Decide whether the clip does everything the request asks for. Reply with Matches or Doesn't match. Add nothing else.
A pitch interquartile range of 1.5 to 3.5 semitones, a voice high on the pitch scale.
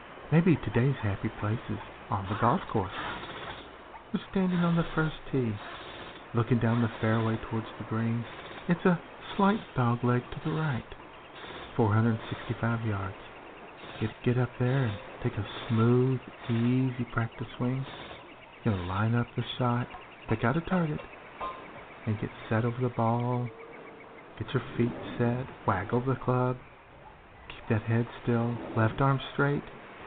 Doesn't match